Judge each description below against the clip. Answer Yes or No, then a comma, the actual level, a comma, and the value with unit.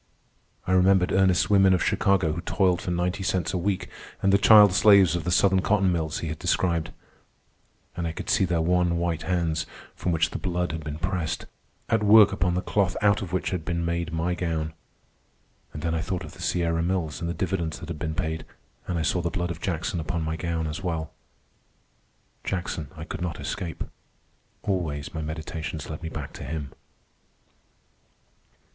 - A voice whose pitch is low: Yes, very low, 85 Hz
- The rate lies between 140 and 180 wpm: No, average, 195 wpm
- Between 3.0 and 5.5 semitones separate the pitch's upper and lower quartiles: No, narrow, 2.5 semitones